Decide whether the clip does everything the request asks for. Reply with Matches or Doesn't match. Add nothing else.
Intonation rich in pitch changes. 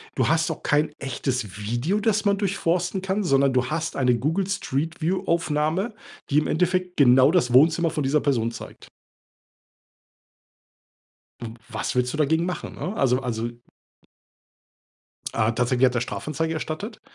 Matches